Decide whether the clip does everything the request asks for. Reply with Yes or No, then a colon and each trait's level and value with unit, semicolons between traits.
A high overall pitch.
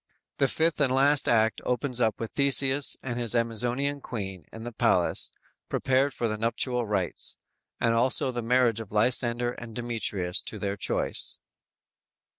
No: low, 120 Hz